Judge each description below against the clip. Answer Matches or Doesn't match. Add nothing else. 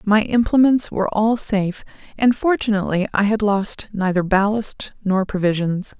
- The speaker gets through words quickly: Doesn't match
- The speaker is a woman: Matches